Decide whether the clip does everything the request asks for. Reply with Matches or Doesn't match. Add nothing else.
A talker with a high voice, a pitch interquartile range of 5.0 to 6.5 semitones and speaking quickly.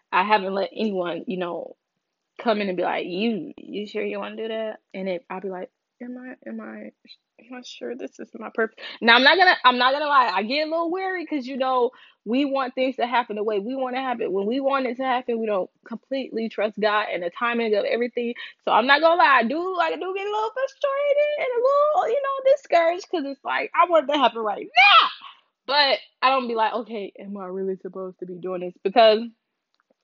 Matches